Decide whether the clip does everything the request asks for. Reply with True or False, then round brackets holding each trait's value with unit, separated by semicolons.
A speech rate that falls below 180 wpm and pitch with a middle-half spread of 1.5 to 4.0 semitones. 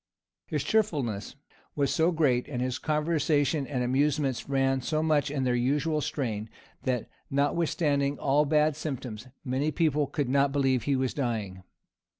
True (150 wpm; 2.8 semitones)